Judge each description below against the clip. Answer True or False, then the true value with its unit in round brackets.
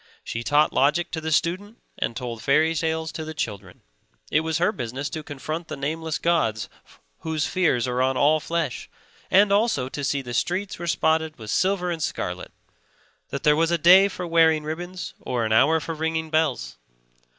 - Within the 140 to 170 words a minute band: False (185 wpm)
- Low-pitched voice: False (155 Hz)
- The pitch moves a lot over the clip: False (3.9 semitones)